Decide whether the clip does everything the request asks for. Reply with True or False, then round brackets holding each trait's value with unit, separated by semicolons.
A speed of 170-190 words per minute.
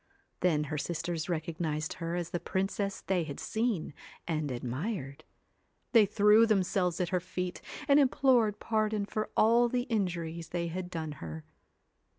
False (155 wpm)